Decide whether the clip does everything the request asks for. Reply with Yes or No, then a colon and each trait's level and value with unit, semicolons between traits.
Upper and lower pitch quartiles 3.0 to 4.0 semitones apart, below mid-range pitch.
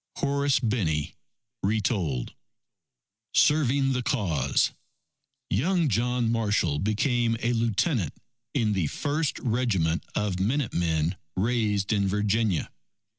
No: average, 4.8 semitones; low, 110 Hz